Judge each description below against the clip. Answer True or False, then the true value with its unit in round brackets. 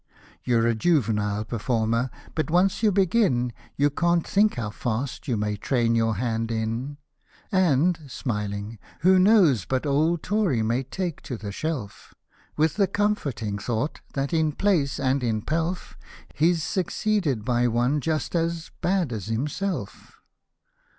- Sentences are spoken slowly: False (145 wpm)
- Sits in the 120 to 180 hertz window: True (140 Hz)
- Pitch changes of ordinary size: False (7.1 semitones)